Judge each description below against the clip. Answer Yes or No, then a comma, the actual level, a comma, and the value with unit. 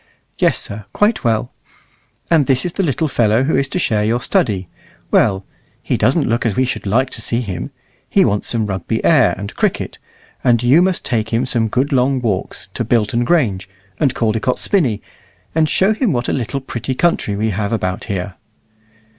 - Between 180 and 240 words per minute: Yes, average, 190 wpm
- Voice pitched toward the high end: No, low, 120 Hz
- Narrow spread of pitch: No, average, 4.4 semitones